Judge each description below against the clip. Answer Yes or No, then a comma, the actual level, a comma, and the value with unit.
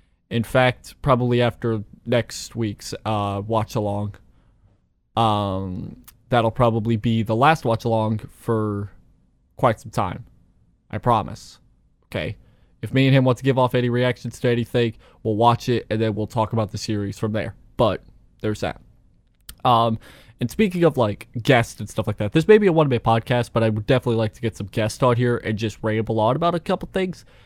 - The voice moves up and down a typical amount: No, narrow, 2.2 semitones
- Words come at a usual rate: Yes, average, 190 wpm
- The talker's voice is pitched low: Yes, low, 115 Hz